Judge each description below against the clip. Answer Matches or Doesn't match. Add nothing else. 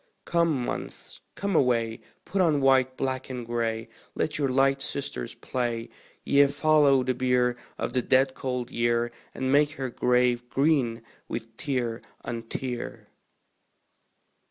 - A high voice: Doesn't match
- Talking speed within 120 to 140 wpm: Matches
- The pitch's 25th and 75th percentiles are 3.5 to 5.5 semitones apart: Doesn't match